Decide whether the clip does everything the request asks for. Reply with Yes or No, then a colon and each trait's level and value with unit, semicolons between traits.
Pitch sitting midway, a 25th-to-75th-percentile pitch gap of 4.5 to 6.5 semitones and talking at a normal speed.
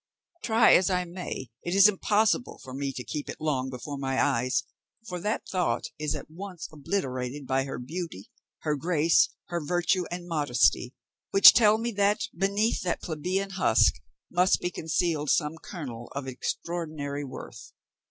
Yes: medium, 165 Hz; average, 5.3 semitones; average, 160 wpm